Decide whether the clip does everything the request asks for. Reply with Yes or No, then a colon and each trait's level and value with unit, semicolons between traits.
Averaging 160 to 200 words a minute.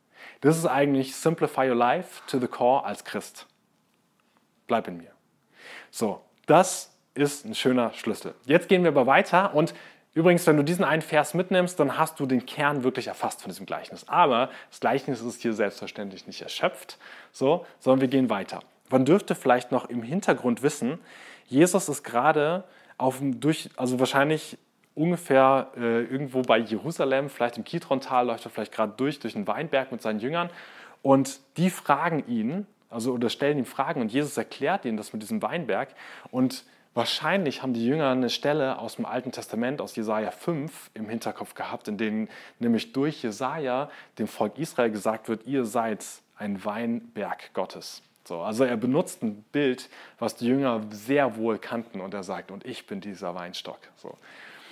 Yes: average, 175 wpm